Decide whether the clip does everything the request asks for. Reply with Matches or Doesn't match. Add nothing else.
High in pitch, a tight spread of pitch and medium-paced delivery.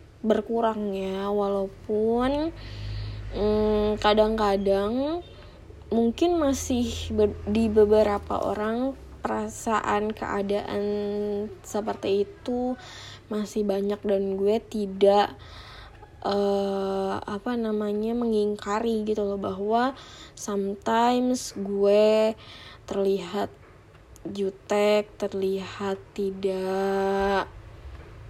Doesn't match